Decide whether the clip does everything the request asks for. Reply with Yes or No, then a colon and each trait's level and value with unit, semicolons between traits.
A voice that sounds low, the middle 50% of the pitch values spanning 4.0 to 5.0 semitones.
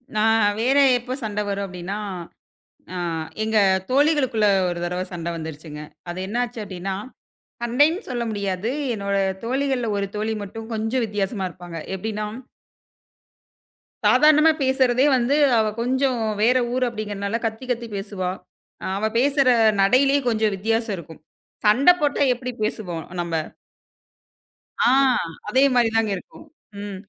No: high, 220 Hz; average, 4.3 semitones